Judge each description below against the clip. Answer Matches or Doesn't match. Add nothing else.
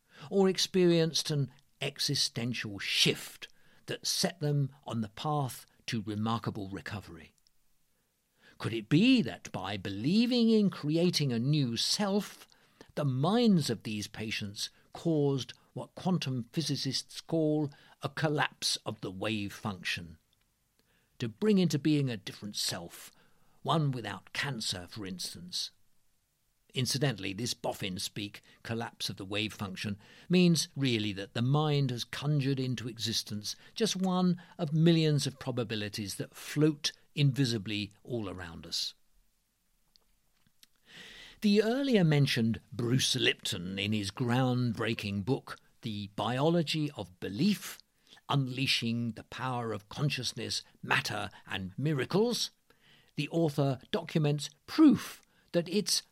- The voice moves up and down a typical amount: Doesn't match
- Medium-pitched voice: Doesn't match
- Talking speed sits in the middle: Doesn't match